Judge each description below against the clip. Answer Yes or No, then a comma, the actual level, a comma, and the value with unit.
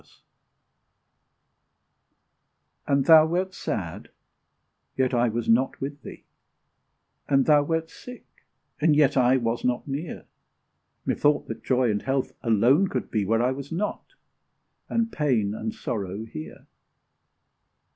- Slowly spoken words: Yes, slow, 125 wpm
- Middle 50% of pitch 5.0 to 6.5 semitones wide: No, average, 4.6 semitones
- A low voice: Yes, low, 130 Hz